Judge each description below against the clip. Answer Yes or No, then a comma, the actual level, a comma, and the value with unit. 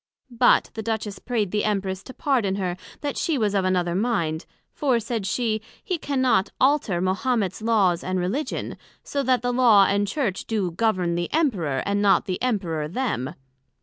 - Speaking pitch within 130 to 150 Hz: No, high, 205 Hz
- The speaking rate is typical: Yes, average, 175 wpm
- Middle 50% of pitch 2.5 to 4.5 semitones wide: No, average, 4.9 semitones